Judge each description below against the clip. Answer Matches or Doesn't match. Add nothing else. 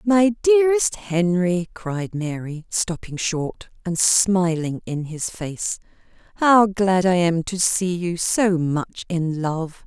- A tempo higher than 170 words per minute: Doesn't match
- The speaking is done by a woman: Matches